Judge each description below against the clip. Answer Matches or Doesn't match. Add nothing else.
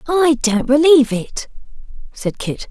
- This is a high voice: Matches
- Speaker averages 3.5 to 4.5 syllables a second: Matches